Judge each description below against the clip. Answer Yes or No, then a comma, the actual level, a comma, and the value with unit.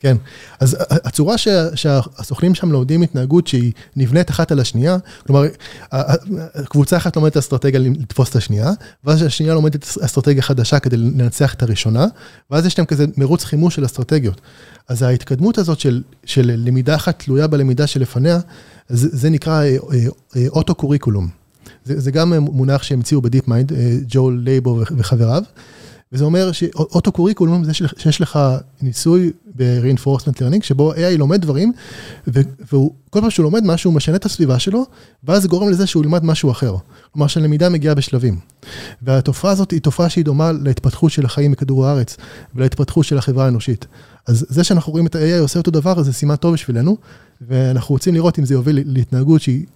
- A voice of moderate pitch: Yes, medium, 145 Hz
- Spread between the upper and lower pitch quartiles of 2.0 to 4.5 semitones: Yes, average, 4.1 semitones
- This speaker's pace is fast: Yes, fast, 160 wpm